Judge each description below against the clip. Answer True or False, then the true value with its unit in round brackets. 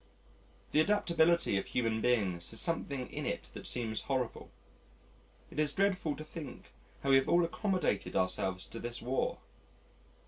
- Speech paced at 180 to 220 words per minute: False (150 wpm)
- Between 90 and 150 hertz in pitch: True (135 Hz)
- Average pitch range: False (6.8 semitones)